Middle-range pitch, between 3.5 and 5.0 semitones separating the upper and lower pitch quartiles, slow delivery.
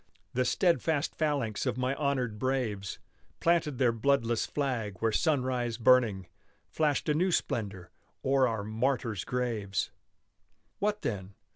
No: low, 125 Hz; average, 4.2 semitones; slow, 125 wpm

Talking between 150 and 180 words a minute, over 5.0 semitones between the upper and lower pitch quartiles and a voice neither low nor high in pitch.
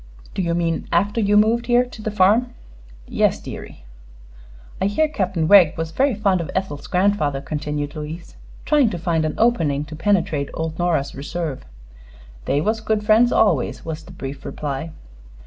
Yes: average, 165 wpm; wide, 5.5 semitones; medium, 175 Hz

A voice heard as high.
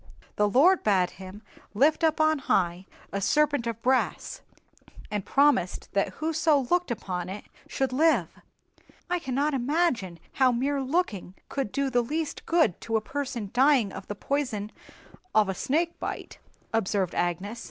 Yes: very high, 250 Hz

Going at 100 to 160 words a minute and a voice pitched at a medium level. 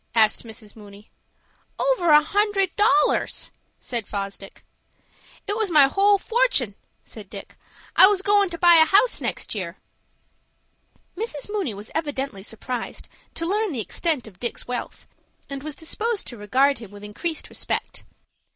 No: average, 150 wpm; very high, 295 Hz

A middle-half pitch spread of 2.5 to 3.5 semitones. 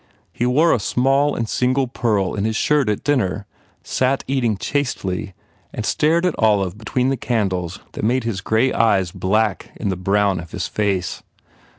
No: average, 4.8 semitones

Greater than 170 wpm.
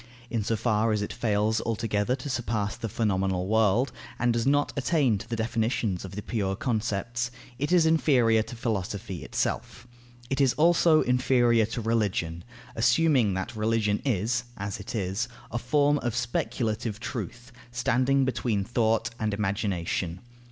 No: average, 150 wpm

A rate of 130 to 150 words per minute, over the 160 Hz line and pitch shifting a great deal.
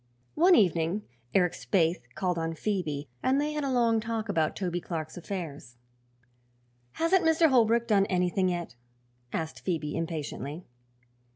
Yes: slow, 135 wpm; medium, 185 Hz; wide, 5.9 semitones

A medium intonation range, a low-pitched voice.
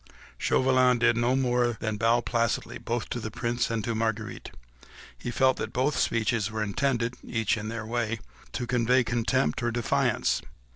No: narrow, 1.7 semitones; low, 120 Hz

